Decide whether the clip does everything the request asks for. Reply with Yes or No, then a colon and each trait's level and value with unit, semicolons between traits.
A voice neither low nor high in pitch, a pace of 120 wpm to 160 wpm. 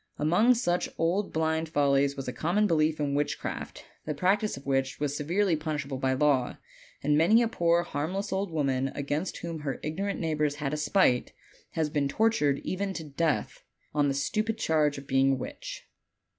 No: medium, 155 Hz; average, 180 wpm